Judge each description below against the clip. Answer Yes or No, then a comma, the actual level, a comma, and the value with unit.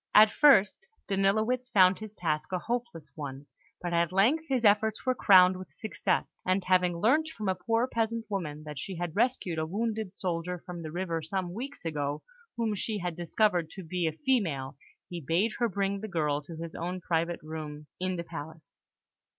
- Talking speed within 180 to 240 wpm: Yes, average, 190 wpm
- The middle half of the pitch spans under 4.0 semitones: No, average, 4.7 semitones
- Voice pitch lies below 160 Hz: No, medium, 185 Hz